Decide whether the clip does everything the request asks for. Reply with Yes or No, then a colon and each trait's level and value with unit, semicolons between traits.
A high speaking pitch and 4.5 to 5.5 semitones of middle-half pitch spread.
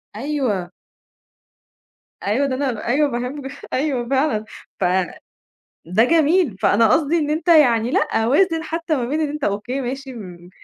Yes: very high, 265 Hz; average, 5.0 semitones